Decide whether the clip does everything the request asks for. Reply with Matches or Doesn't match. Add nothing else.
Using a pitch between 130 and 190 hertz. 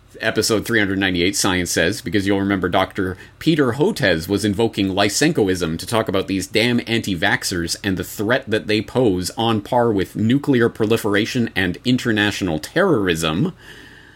Doesn't match